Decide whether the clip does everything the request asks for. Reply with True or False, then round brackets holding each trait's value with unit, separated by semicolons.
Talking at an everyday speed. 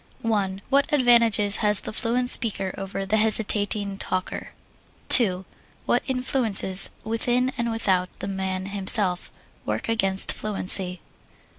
False (115 wpm)